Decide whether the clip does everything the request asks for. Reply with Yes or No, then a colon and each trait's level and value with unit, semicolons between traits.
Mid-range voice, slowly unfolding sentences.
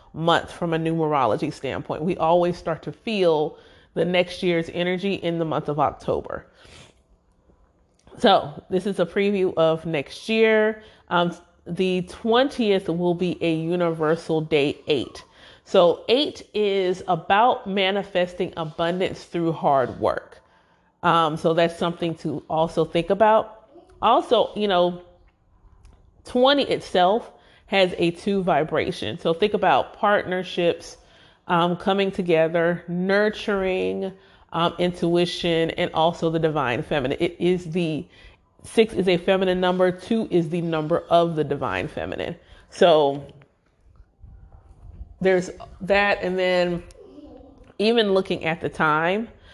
Yes: medium, 175 Hz; slow, 125 wpm